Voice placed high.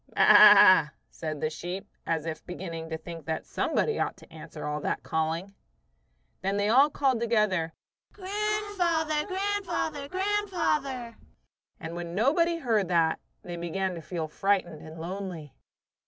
Yes: high, 195 Hz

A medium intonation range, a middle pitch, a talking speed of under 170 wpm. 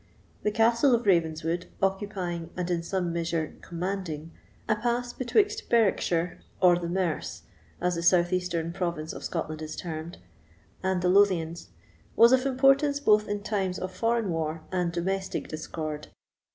Yes: average, 3.9 semitones; medium, 180 Hz; average, 145 wpm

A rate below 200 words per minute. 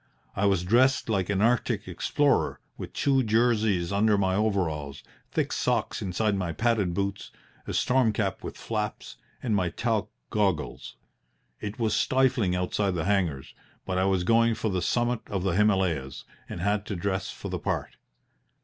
Yes: average, 165 wpm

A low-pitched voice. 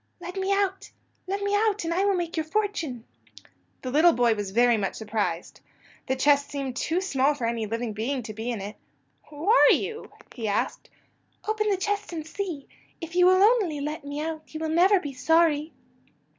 No: very high, 310 Hz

